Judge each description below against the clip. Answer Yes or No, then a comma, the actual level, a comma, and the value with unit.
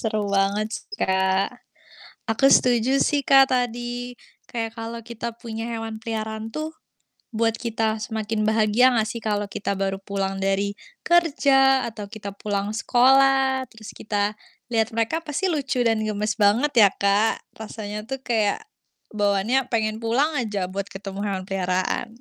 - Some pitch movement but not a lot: Yes, average, 3.2 semitones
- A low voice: No, high, 220 Hz